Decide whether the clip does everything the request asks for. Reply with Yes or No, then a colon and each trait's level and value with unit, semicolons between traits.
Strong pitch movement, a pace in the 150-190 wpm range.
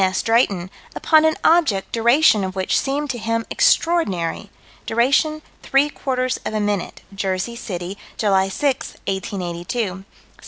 No: wide, 6.2 semitones; average, 140 wpm